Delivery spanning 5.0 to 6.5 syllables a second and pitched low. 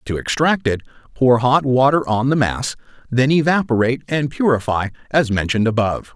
Yes: 5.5 syllables/s; low, 125 Hz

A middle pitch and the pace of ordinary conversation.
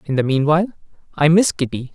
Yes: medium, 155 Hz; average, 185 wpm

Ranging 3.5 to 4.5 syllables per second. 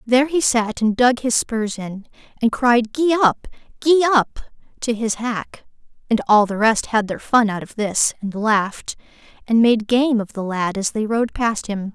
Yes: 4.4 syllables/s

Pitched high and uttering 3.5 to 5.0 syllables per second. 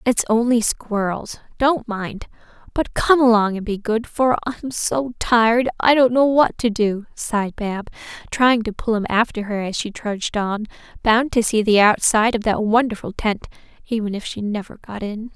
Yes: high, 225 Hz; 4.8 syllables/s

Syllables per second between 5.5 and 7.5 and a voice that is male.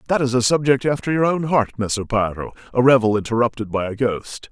Yes: 5.9 syllables/s; male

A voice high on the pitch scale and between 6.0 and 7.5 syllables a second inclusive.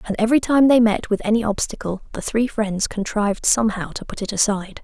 Yes: high, 215 Hz; 6.2 syllables/s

